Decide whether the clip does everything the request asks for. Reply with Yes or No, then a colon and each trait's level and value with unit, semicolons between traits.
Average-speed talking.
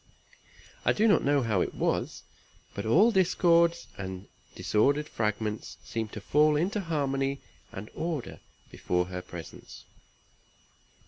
No: slow, 125 wpm